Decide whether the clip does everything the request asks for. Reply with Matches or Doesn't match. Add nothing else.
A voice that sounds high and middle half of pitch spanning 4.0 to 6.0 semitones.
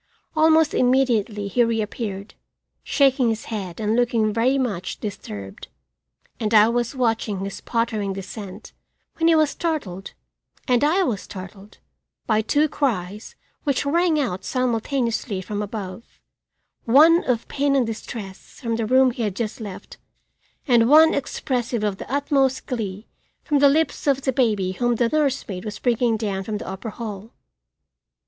Matches